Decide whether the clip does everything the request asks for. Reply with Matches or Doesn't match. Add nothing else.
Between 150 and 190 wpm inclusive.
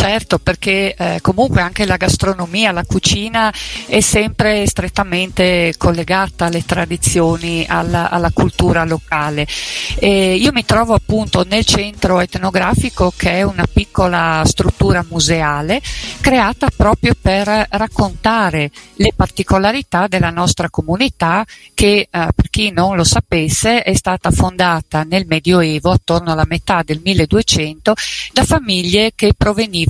Doesn't match